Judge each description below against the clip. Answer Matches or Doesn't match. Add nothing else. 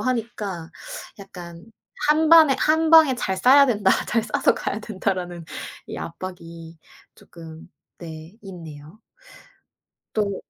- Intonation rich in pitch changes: Matches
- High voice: Matches